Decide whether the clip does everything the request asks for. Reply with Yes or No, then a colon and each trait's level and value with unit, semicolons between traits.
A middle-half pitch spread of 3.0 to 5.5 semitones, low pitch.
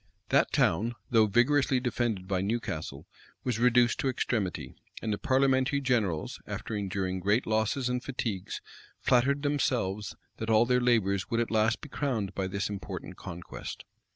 Yes: average, 4.2 semitones; low, 115 Hz